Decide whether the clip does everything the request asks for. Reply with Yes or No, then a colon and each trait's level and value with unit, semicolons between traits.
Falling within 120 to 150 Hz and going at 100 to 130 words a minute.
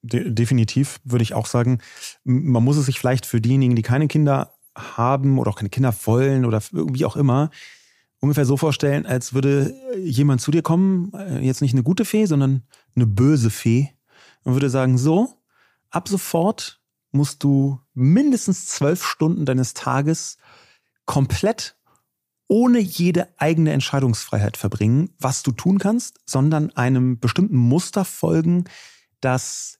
No: low, 135 Hz; average, 145 wpm